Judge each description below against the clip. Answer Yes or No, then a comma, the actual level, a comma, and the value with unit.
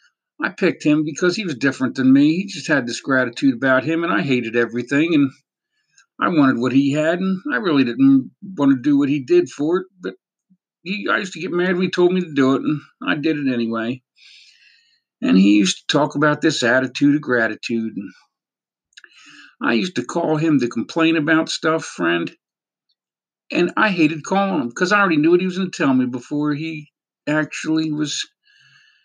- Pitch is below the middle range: No, medium, 155 Hz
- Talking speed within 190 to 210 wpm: Yes, average, 200 wpm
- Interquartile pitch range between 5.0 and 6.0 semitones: Yes, wide, 5.5 semitones